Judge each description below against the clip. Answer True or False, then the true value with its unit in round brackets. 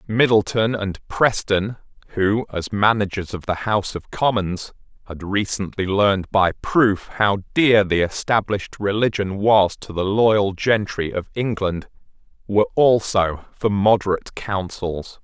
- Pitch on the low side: True (100 Hz)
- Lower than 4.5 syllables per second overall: True (4.1 syllables/s)